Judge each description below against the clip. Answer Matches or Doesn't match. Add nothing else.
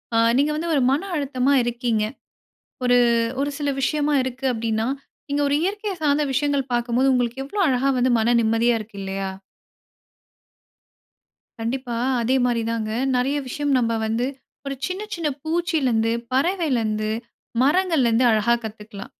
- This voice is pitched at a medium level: Doesn't match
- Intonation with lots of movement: Doesn't match